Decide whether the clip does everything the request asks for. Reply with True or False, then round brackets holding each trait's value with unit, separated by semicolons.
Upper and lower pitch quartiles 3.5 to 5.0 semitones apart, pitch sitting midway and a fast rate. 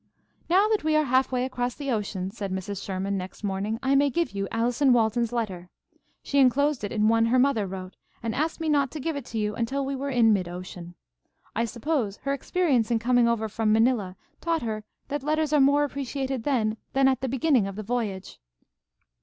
False (4.7 semitones; 240 Hz; 210 wpm)